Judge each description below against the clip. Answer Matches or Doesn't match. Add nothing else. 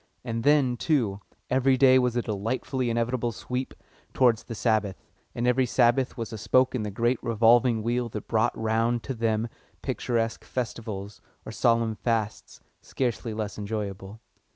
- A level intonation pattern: Matches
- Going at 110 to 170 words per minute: Matches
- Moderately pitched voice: Doesn't match